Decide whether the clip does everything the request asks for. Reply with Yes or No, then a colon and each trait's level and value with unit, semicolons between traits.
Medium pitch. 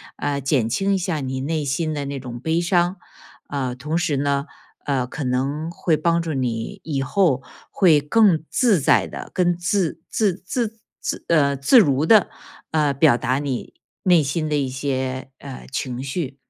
Yes: medium, 145 Hz